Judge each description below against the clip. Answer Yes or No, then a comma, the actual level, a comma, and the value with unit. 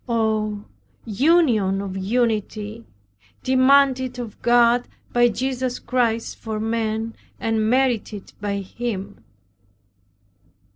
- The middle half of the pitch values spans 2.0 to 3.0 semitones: Yes, average, 2.7 semitones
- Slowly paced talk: Yes, slow, 90 wpm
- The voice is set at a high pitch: Yes, high, 230 Hz